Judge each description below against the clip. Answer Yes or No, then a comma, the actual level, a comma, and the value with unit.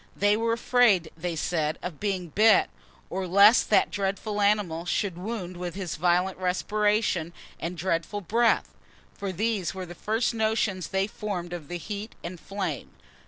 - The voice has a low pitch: No, high, 190 Hz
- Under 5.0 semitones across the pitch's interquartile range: Yes, average, 3.2 semitones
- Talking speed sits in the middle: Yes, average, 160 wpm